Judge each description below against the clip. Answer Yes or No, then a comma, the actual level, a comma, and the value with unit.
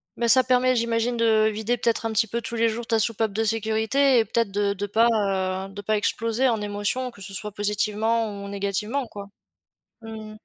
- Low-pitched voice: No, high, 220 Hz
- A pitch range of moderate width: No, narrow, 2.1 semitones